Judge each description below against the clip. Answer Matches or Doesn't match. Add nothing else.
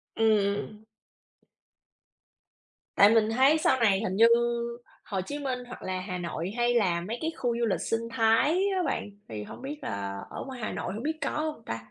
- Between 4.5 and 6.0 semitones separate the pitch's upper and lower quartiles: Matches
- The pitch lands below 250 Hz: Matches